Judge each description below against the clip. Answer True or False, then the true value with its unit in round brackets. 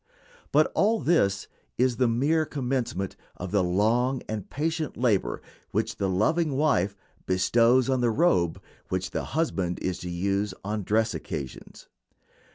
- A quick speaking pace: False (145 wpm)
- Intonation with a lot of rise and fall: True (6.1 semitones)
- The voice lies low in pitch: True (110 Hz)